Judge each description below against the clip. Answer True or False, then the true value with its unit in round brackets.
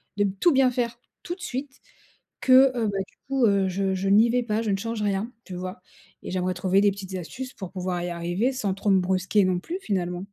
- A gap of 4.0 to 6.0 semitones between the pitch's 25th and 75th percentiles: True (4.4 semitones)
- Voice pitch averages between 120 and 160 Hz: False (200 Hz)